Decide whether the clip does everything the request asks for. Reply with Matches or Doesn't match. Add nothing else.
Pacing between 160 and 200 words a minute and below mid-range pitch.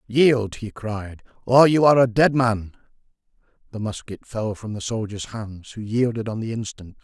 Matches